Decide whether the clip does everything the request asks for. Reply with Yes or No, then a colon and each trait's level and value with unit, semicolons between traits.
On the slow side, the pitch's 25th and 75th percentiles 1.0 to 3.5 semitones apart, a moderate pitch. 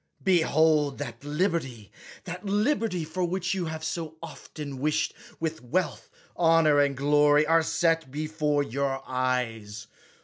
Yes: slow, 130 wpm; average, 2.9 semitones; medium, 155 Hz